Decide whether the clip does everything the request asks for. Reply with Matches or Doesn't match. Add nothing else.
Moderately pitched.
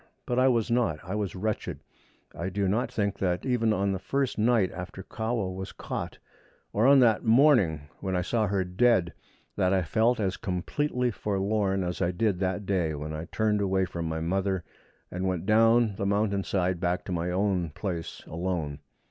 Doesn't match